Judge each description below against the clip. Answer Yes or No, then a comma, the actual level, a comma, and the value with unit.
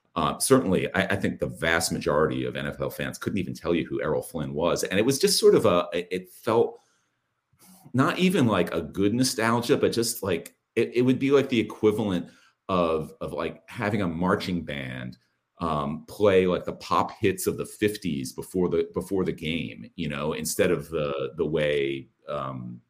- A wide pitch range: Yes, wide, 6.8 semitones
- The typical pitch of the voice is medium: No, very low, 95 Hz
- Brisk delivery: No, average, 190 wpm